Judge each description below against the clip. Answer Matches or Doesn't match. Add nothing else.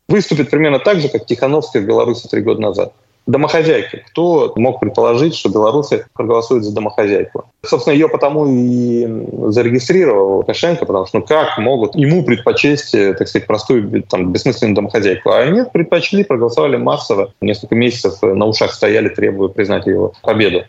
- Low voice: Doesn't match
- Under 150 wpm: Doesn't match